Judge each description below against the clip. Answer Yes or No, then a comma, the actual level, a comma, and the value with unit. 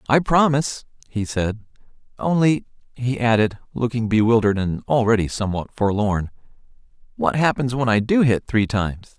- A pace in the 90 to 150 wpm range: Yes, slow, 135 wpm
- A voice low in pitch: Yes, low, 115 Hz